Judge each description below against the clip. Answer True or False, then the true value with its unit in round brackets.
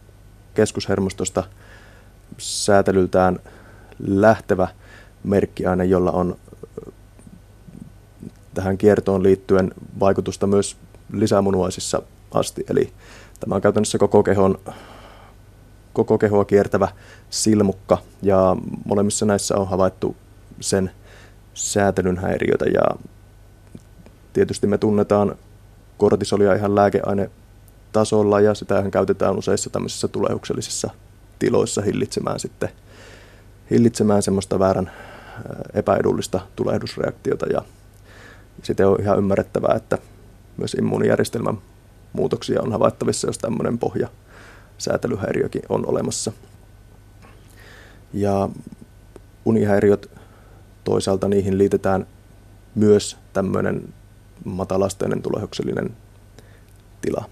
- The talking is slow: True (80 wpm)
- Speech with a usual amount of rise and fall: False (1.2 semitones)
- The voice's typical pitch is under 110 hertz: True (100 Hz)